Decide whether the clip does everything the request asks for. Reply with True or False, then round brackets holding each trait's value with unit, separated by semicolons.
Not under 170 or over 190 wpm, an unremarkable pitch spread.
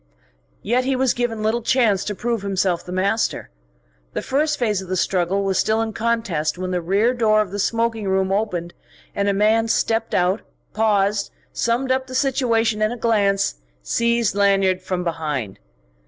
True (175 wpm; 3.5 semitones)